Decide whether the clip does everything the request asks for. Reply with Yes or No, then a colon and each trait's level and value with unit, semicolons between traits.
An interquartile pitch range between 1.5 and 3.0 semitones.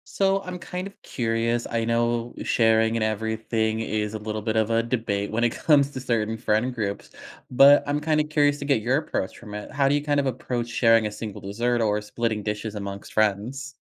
No: average, 4.0 semitones